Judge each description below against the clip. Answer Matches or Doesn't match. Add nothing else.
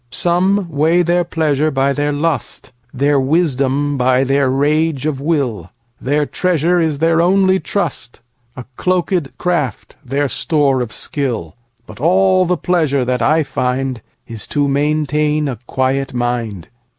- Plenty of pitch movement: Doesn't match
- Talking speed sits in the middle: Doesn't match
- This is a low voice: Doesn't match